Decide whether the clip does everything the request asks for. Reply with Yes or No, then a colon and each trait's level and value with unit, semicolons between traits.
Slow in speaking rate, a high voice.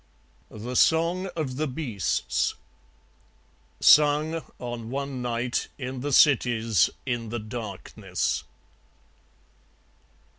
No: slow, 85 wpm; low, 125 Hz